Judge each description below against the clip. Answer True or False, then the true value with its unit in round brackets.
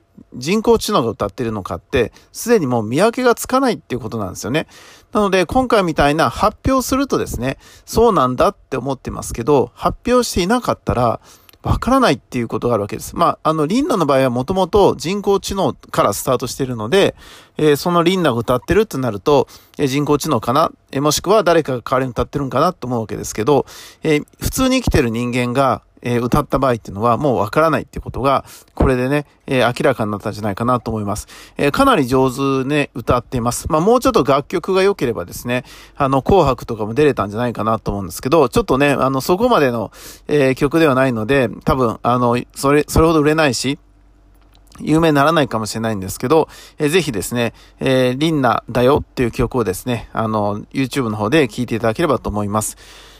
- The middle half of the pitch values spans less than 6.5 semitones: True (5.5 semitones)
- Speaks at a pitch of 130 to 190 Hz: True (135 Hz)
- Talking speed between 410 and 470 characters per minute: True (460 characters per minute)